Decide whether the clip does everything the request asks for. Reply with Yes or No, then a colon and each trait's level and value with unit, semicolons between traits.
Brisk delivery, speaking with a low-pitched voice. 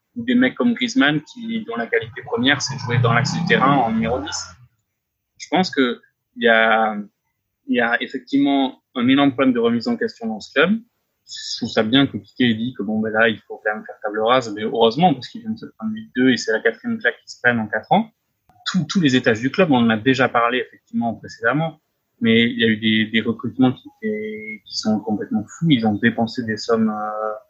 Yes: fast, 235 wpm; low, 130 Hz